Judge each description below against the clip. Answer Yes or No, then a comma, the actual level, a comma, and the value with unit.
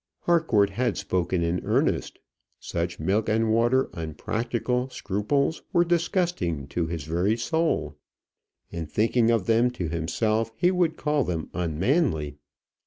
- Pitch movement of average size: No, wide, 7.4 semitones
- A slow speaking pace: Yes, slow, 130 wpm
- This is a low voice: Yes, low, 110 Hz